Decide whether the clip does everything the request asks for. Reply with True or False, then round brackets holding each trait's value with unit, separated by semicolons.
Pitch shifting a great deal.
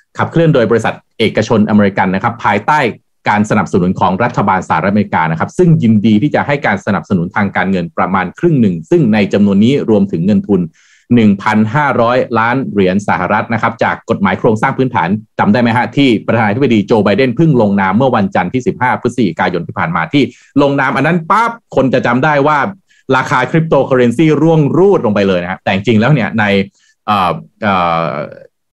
True (7.6 semitones)